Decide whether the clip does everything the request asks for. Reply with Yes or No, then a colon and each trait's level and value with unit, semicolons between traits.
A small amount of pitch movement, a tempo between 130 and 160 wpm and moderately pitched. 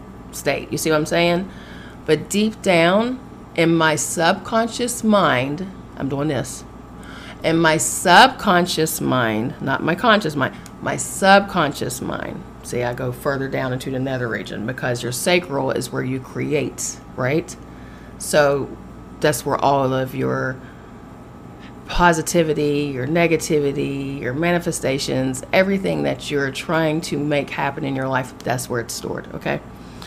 No: average, 4.7 semitones; average, 140 wpm; medium, 145 Hz